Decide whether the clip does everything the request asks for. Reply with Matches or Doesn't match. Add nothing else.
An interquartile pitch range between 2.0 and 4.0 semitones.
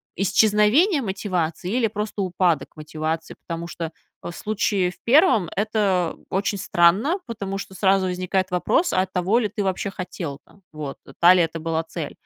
Matches